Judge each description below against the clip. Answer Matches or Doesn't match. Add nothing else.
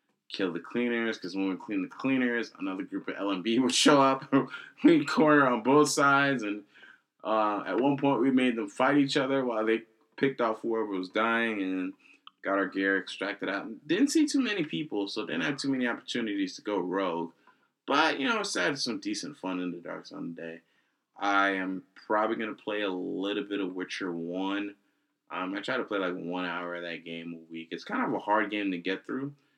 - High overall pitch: Doesn't match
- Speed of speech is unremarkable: Doesn't match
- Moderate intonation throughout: Doesn't match